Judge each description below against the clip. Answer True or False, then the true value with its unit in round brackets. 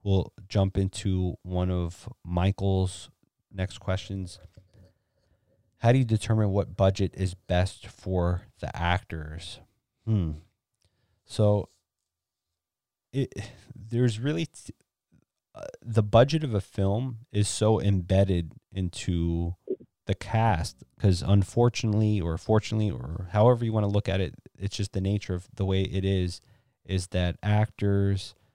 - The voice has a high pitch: False (100 Hz)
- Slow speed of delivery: True (130 wpm)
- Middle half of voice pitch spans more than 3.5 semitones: False (3.1 semitones)